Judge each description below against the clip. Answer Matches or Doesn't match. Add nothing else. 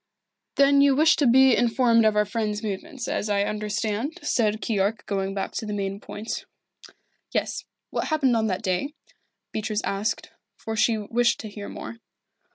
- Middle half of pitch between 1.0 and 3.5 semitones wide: Matches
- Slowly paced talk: Doesn't match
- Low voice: Doesn't match